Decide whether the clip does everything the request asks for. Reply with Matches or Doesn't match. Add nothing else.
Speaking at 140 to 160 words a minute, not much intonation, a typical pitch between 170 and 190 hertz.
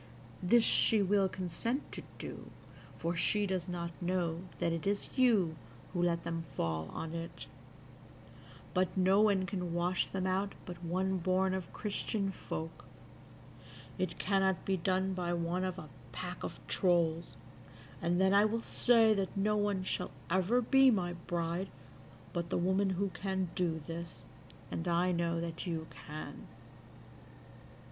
Matches